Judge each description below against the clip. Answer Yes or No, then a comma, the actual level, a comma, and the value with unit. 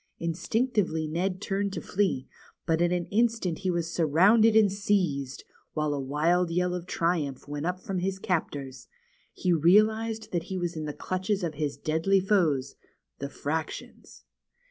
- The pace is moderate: Yes, average, 160 wpm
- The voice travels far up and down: No, average, 3.8 semitones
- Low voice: No, medium, 175 Hz